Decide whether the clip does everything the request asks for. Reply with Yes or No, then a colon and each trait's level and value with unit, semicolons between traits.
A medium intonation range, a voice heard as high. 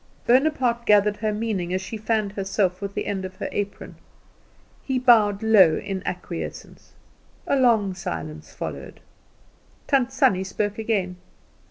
Yes: average, 3.2 semitones; high, 205 Hz